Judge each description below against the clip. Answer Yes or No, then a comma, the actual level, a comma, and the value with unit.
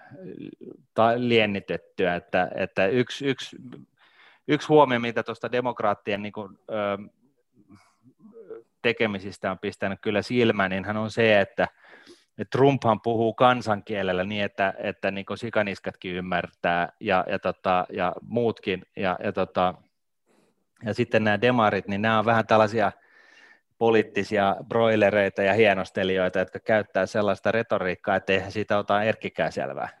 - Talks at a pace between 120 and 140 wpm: Yes, average, 125 wpm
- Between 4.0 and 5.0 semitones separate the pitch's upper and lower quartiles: No, average, 2.9 semitones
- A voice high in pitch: No, low, 105 Hz